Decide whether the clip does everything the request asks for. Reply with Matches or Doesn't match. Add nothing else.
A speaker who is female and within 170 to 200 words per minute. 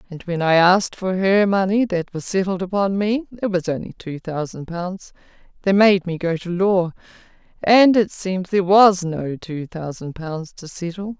Matches